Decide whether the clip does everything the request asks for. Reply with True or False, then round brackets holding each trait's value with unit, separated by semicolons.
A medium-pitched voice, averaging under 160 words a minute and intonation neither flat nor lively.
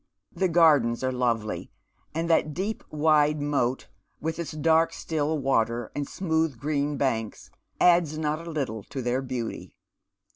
True (150 Hz; 145 wpm; 3.9 semitones)